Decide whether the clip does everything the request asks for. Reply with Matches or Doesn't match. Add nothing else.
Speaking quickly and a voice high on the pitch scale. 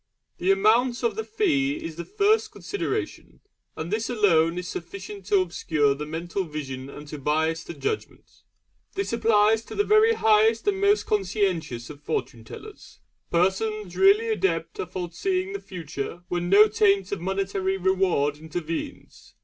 Doesn't match